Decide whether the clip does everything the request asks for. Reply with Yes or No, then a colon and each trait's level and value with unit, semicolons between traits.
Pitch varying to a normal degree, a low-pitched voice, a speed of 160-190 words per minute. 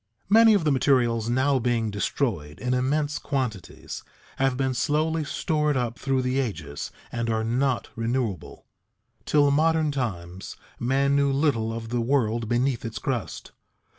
No: average, 3.6 semitones; low, 130 Hz; average, 150 wpm